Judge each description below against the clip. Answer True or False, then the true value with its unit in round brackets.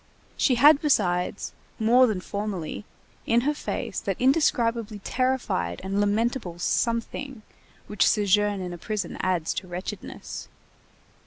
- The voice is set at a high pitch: True (210 Hz)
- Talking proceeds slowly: True (125 wpm)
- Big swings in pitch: False (4.6 semitones)